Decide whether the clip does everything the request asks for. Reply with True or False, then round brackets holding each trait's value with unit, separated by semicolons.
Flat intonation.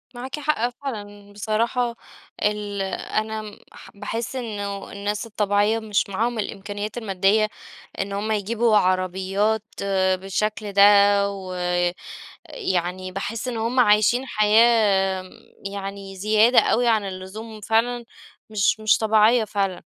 True (2.2 semitones)